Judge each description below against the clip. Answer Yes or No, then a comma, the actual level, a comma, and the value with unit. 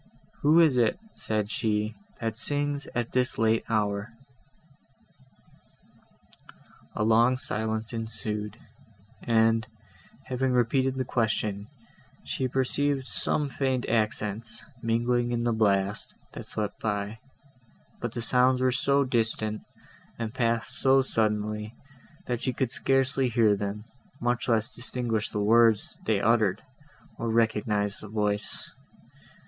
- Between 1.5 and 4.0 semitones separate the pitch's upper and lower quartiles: Yes, average, 2.8 semitones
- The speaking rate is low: Yes, slow, 120 wpm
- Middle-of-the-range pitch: No, low, 115 Hz